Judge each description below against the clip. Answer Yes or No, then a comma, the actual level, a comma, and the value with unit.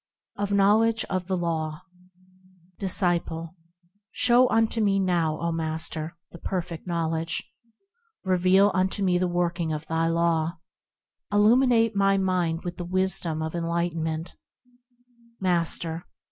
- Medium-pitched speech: Yes, medium, 175 Hz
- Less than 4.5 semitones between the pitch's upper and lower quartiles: Yes, average, 2.8 semitones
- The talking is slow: Yes, slow, 120 wpm